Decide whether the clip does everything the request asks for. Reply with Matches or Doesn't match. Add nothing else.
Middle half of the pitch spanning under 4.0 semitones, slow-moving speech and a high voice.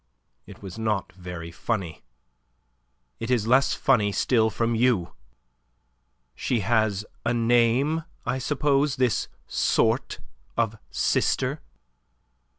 Doesn't match